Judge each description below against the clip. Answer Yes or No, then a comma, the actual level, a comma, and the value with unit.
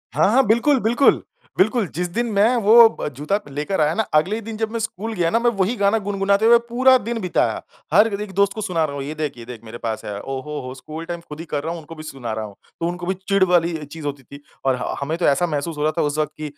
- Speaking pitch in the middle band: Yes, medium, 175 Hz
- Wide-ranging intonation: Yes, wide, 6.6 semitones